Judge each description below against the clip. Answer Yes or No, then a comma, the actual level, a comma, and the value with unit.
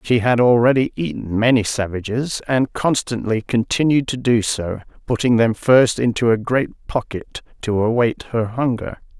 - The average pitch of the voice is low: Yes, low, 120 Hz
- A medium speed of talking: Yes, average, 150 wpm